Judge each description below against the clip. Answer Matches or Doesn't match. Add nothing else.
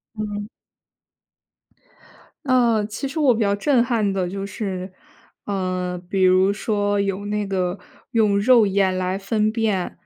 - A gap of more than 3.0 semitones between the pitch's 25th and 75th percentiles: Doesn't match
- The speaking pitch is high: Matches